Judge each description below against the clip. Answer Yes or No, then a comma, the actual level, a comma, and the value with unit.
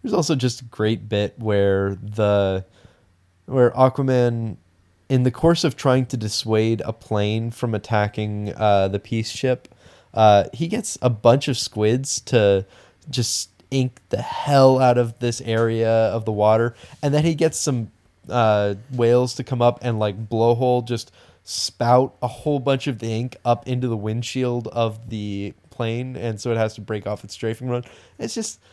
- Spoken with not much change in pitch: No, average, 3.1 semitones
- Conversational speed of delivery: Yes, average, 175 wpm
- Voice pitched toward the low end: Yes, low, 115 Hz